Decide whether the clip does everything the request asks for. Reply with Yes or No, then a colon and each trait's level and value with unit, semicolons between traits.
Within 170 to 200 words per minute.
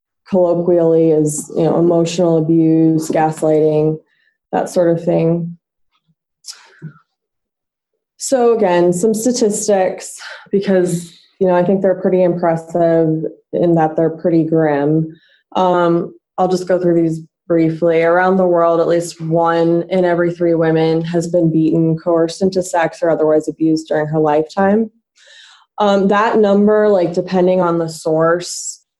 No: slow, 135 wpm